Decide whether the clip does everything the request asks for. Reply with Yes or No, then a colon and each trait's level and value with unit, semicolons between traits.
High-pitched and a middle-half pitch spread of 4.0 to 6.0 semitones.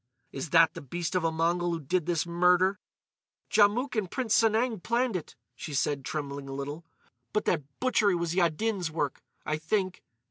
No: medium, 175 Hz; average, 4.8 semitones